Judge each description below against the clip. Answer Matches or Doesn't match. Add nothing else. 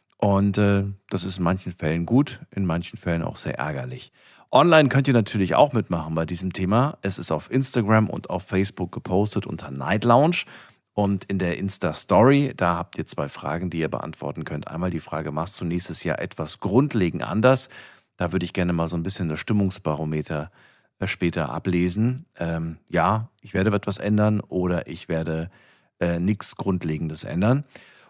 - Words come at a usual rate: Matches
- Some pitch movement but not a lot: Matches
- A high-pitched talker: Doesn't match